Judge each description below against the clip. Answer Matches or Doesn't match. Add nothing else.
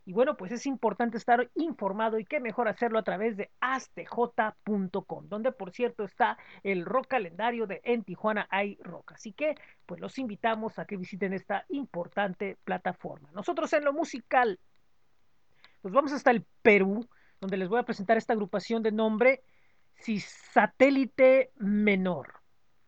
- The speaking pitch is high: Matches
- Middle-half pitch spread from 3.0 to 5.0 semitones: Matches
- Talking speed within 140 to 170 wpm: Matches